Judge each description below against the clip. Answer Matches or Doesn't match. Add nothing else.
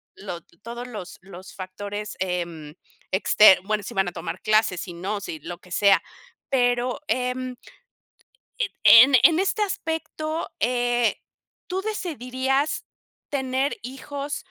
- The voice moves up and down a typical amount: Doesn't match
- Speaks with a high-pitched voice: Matches